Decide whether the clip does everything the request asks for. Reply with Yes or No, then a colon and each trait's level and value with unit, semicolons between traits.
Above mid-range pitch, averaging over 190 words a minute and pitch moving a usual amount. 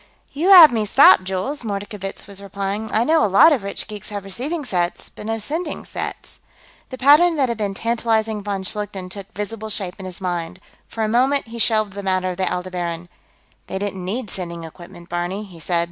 Yes: high, 205 Hz; fast, 205 wpm; average, 3.6 semitones